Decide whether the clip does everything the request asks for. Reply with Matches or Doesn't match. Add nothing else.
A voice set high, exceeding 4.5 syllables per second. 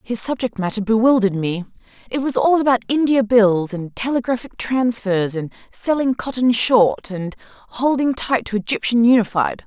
Matches